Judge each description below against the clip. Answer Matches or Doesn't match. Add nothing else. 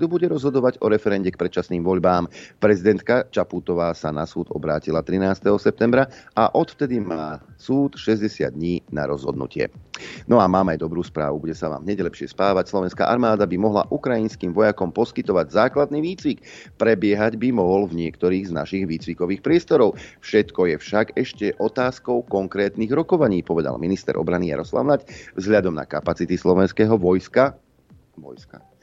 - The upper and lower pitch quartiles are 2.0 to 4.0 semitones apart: Doesn't match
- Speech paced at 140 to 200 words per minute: Matches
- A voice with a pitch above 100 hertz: Doesn't match